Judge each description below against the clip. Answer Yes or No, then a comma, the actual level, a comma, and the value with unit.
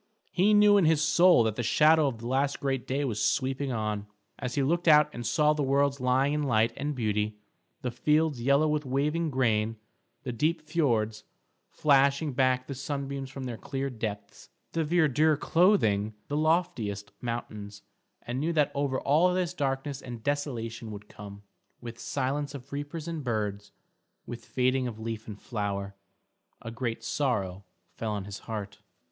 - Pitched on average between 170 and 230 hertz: No, low, 135 Hz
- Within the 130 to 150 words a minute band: No, average, 170 wpm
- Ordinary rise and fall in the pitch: Yes, average, 4.8 semitones